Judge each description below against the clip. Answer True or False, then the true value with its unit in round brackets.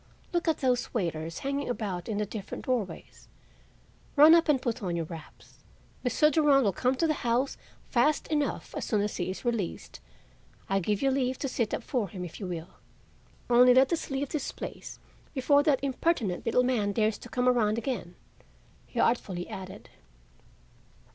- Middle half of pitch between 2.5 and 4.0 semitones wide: False (5.3 semitones)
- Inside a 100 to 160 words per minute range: False (180 wpm)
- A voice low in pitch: False (245 Hz)